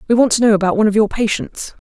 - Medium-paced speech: No, fast, 290 wpm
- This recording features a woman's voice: Yes, female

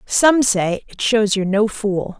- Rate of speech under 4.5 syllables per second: Yes, 3.9 syllables/s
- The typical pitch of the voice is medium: No, high, 210 Hz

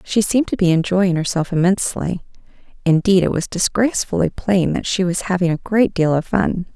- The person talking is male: No, female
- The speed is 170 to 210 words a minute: Yes, average, 185 wpm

